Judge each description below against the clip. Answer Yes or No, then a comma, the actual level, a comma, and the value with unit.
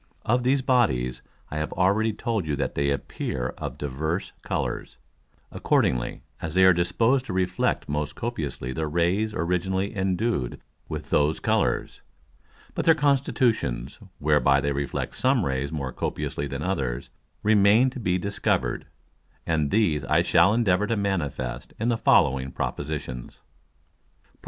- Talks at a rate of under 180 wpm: Yes, average, 140 wpm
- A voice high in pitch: No, very low, 85 Hz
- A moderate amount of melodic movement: No, wide, 7.2 semitones